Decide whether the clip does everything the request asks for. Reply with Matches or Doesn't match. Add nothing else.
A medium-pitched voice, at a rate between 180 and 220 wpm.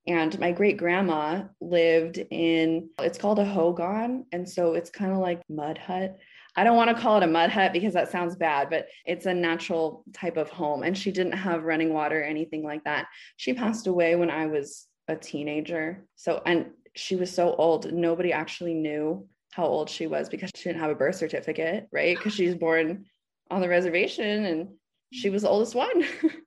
Matches